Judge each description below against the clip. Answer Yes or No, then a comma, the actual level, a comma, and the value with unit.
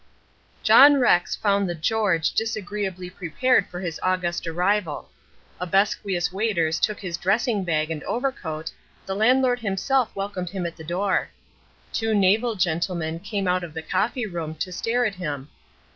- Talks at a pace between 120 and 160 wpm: Yes, average, 150 wpm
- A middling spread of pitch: Yes, average, 3.9 semitones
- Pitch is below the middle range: No, medium, 185 Hz